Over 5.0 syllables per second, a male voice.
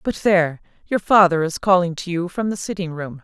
No: 5.5 syllables/s; female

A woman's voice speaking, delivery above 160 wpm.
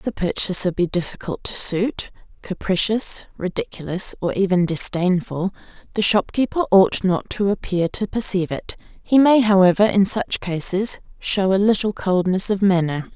No: female; average, 150 wpm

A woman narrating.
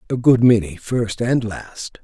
No: male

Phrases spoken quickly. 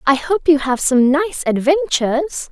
No: average, 165 wpm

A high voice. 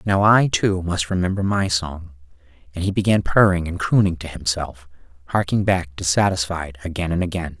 No: very low, 85 Hz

